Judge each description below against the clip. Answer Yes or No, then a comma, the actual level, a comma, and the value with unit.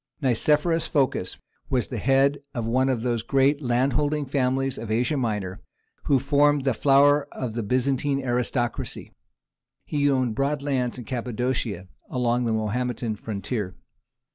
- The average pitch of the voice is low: Yes, low, 130 Hz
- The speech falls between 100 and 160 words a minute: Yes, average, 140 wpm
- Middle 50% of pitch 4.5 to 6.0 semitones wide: No, average, 2.9 semitones